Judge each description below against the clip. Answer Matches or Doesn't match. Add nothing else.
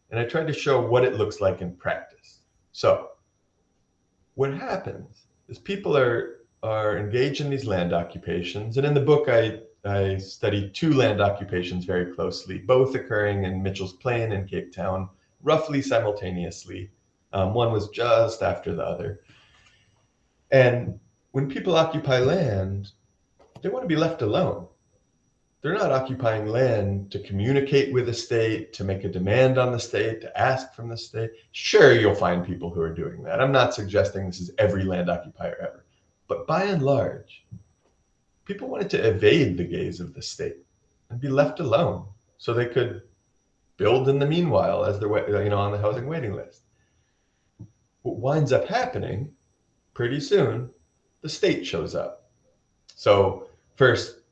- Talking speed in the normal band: Matches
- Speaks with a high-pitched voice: Doesn't match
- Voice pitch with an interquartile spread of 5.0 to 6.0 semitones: Matches